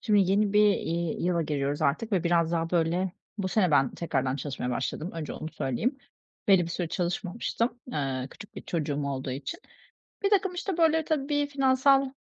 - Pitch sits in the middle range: Yes, medium, 175 Hz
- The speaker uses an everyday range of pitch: No, wide, 8.0 semitones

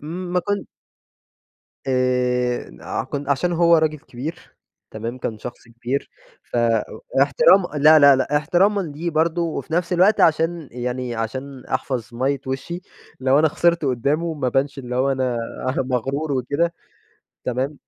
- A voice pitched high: No, medium, 140 Hz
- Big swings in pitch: No, average, 4.4 semitones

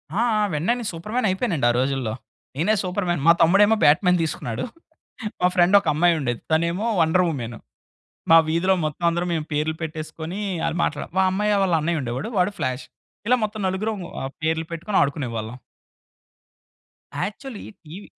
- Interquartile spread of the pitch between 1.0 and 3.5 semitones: No, average, 4.2 semitones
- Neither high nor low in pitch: Yes, medium, 170 Hz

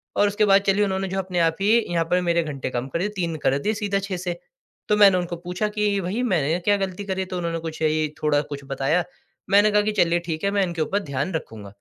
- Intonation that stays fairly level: No, average, 3.7 semitones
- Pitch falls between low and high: Yes, medium, 180 Hz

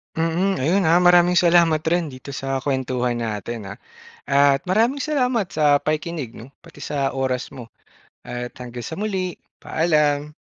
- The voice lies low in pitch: No, medium, 150 Hz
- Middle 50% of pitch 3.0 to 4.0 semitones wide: No, average, 5.1 semitones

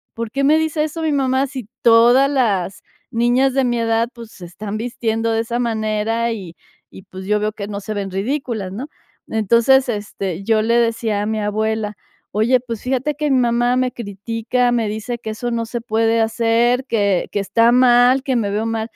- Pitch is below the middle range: No, high, 230 Hz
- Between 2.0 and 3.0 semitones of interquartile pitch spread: Yes, narrow, 2.5 semitones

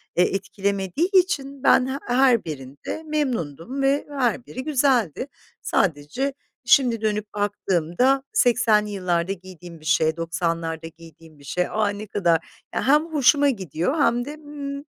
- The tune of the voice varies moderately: No, wide, 8.1 semitones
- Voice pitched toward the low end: No, high, 210 Hz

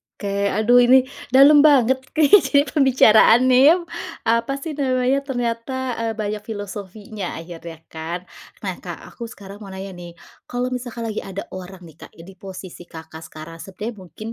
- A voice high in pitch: Yes, high, 215 Hz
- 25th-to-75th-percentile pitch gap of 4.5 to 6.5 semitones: Yes, average, 5.1 semitones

